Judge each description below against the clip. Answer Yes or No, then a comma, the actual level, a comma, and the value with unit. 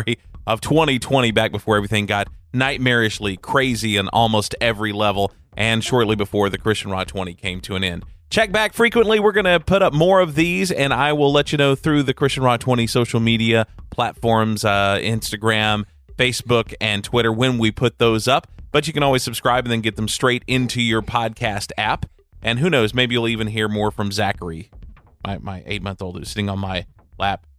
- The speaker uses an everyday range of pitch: Yes, average, 3.9 semitones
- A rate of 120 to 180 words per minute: No, average, 195 wpm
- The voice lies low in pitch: Yes, low, 115 Hz